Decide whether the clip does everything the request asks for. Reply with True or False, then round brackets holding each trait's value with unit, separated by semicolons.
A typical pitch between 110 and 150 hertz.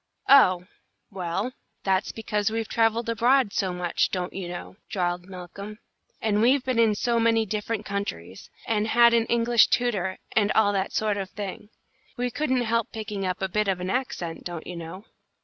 False (210 Hz)